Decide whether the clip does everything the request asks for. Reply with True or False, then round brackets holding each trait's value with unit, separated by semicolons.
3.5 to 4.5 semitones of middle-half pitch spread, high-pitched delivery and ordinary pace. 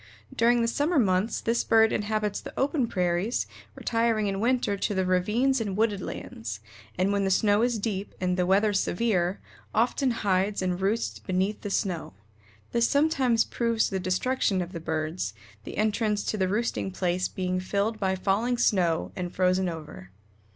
True (3.8 semitones; 200 Hz; 170 wpm)